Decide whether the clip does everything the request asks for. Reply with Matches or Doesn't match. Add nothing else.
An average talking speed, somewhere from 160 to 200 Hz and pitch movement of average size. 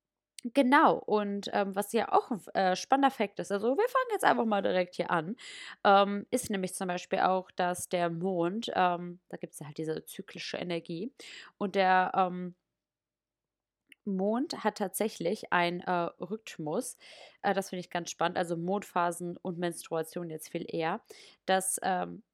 Matches